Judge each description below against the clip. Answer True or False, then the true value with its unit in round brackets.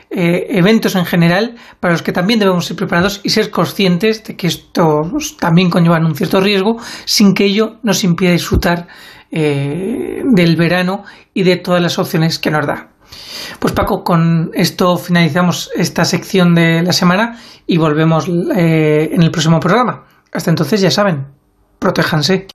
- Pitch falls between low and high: True (180 Hz)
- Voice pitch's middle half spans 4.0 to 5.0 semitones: False (3.0 semitones)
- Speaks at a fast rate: False (160 wpm)